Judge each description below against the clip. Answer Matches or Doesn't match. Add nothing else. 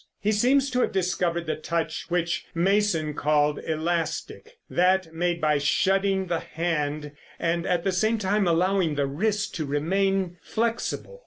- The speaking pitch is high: Doesn't match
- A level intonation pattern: Doesn't match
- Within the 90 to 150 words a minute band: Matches